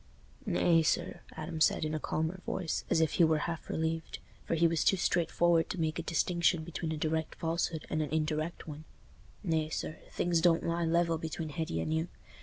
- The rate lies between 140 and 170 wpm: No, average, 190 wpm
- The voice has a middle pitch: Yes, medium, 160 Hz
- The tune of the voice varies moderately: No, narrow, 1.3 semitones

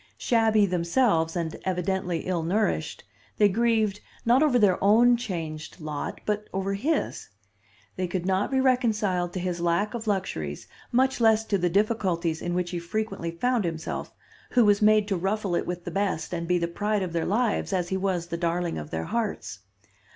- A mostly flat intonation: No, average, 4.0 semitones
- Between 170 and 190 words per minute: Yes, average, 185 wpm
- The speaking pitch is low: No, high, 190 Hz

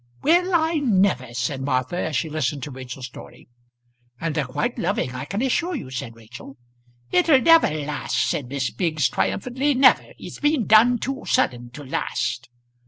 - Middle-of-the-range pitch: Yes, medium, 155 Hz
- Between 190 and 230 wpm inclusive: No, average, 170 wpm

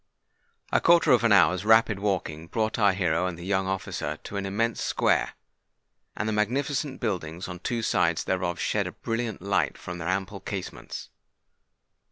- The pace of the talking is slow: No, average, 170 wpm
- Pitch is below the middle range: Yes, low, 100 Hz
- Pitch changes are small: No, average, 3.8 semitones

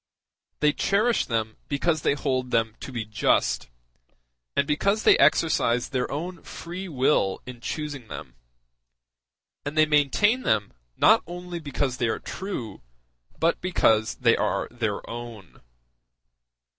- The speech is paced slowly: Yes, slow, 130 wpm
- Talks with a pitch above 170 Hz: No, medium, 140 Hz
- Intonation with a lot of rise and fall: Yes, wide, 6.0 semitones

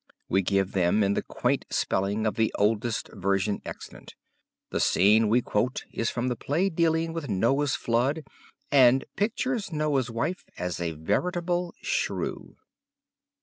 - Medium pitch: No, low, 120 Hz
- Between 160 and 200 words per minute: No, average, 145 wpm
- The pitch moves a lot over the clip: Yes, wide, 7.9 semitones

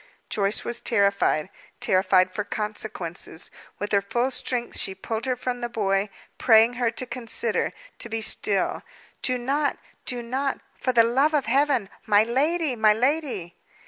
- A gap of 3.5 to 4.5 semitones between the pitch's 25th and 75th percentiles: Yes, average, 3.8 semitones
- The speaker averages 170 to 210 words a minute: No, average, 155 wpm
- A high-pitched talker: Yes, high, 230 Hz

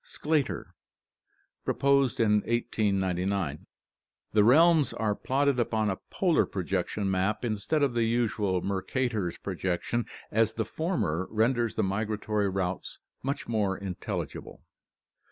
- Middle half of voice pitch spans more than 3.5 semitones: Yes, average, 3.9 semitones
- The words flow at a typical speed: No, slow, 115 wpm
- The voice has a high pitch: No, low, 110 Hz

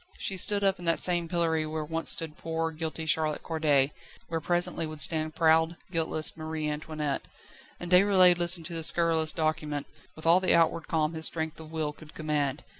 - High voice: No, medium, 160 Hz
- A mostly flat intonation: Yes, narrow, 1.4 semitones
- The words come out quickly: No, average, 190 wpm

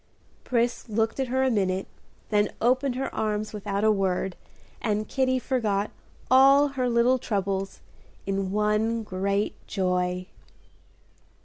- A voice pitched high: Yes, high, 215 Hz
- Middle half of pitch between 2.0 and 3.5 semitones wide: No, average, 4.2 semitones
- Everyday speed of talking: No, slow, 125 wpm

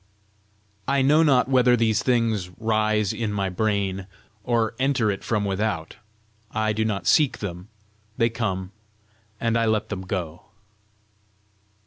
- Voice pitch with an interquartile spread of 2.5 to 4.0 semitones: Yes, average, 3.0 semitones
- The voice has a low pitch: Yes, low, 110 Hz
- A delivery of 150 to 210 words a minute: No, slow, 135 wpm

